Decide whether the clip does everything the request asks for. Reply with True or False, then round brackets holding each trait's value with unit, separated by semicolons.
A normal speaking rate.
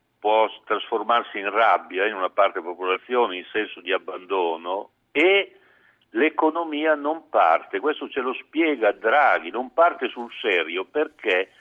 True (135 wpm)